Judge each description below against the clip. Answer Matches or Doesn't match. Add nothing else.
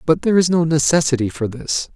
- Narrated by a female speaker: Doesn't match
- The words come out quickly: Matches